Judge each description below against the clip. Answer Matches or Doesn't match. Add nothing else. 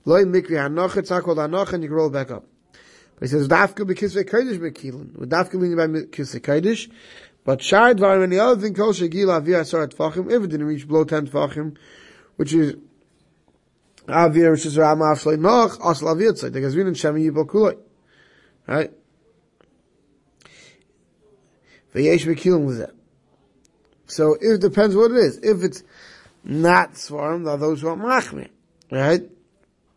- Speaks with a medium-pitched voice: Matches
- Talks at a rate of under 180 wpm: Matches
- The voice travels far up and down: Doesn't match